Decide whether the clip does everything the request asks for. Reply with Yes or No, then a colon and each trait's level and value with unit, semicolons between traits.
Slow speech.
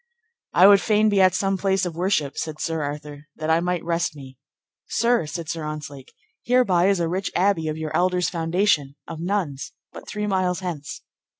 No: average, 190 wpm